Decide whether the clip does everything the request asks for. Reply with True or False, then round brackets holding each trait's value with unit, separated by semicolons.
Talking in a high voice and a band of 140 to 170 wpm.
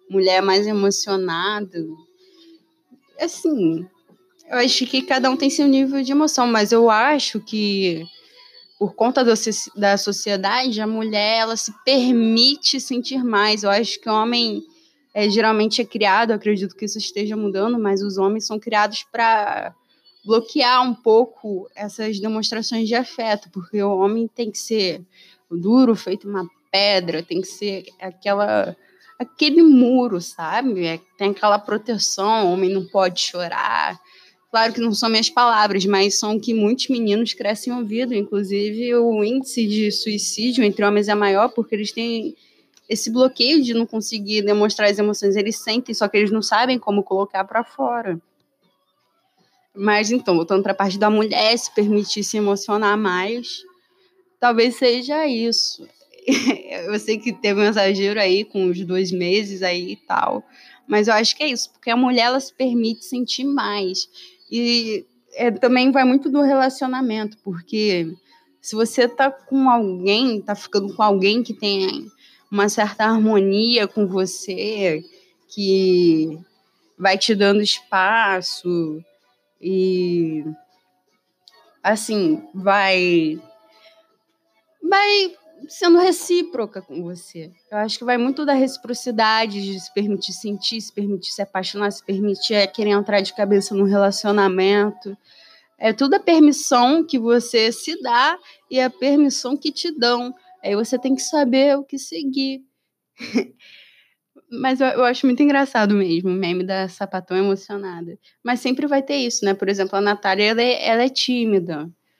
True (215 Hz; 150 wpm)